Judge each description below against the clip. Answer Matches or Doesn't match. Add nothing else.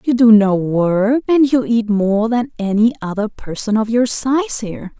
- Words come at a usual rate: Matches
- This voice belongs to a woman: Matches